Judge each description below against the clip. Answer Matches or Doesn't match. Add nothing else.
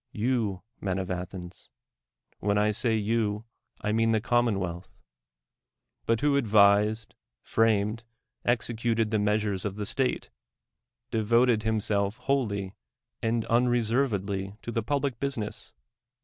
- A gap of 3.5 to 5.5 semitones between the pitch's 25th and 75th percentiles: Doesn't match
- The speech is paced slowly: Matches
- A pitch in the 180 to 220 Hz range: Doesn't match